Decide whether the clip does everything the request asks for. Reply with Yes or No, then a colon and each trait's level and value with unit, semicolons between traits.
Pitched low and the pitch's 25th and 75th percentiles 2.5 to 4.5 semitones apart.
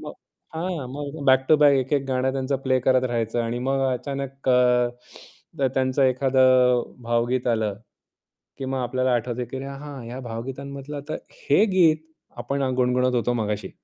No: low, 130 Hz; narrow, 1.9 semitones